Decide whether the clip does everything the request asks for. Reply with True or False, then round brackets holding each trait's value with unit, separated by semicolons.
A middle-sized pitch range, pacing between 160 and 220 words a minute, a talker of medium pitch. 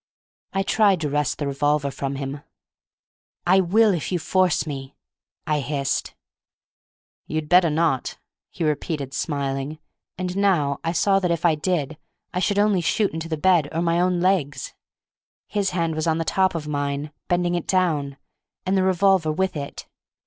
True (4.1 semitones; 170 wpm; 165 Hz)